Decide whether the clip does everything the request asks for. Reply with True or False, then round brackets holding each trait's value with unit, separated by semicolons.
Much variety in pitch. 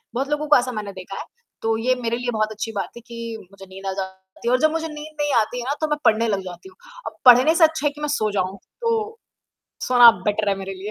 True (6.9 semitones)